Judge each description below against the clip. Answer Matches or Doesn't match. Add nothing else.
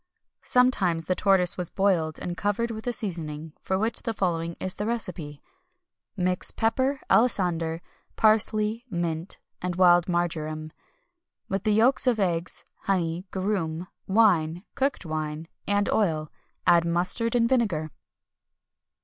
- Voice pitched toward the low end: Doesn't match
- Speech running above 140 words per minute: Doesn't match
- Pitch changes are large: Doesn't match